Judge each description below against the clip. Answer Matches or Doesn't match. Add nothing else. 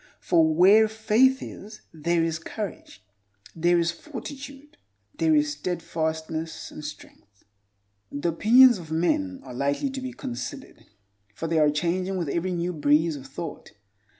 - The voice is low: Doesn't match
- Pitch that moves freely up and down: Matches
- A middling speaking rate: Matches